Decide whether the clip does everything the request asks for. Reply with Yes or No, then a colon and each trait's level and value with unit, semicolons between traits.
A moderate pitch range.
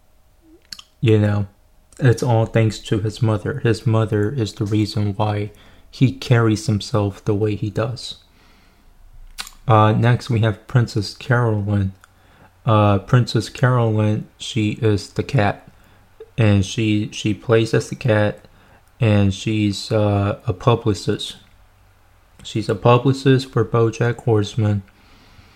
No: narrow, 2.1 semitones